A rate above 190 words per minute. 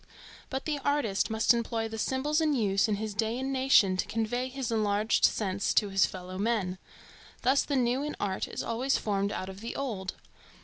Yes: average, 200 wpm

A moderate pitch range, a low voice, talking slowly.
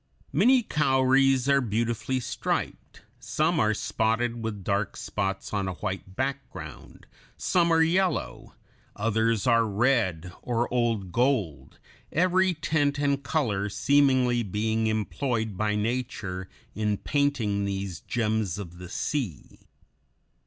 Yes: average, 5.0 semitones; low, 115 Hz; slow, 115 wpm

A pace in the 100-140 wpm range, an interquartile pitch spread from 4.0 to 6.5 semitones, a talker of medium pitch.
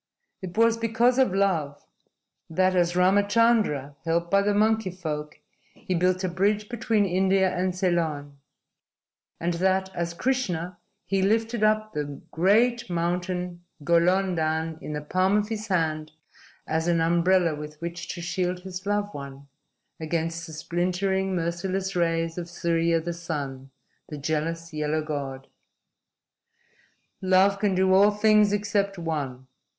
No: slow, 135 wpm; average, 3.3 semitones; medium, 180 Hz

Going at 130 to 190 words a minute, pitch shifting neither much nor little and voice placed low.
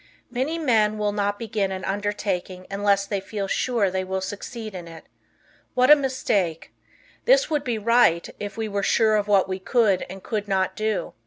No: average, 185 wpm; average, 3.0 semitones; high, 205 Hz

